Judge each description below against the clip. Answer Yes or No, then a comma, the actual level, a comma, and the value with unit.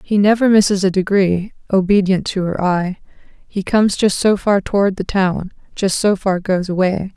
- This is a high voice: Yes, high, 195 Hz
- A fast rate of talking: No, average, 185 wpm